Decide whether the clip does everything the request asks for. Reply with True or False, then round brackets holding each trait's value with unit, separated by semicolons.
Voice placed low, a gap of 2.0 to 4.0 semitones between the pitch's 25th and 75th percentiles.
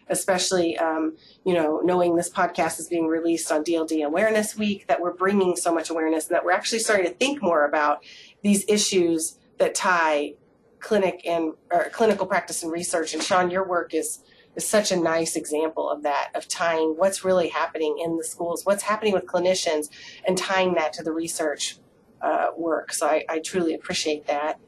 False (170 Hz; 2.7 semitones)